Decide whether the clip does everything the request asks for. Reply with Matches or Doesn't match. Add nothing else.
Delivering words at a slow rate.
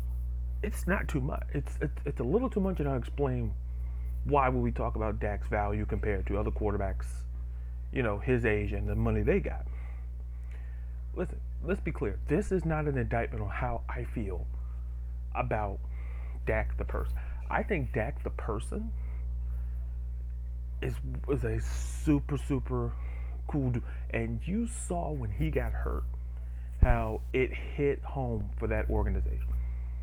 Doesn't match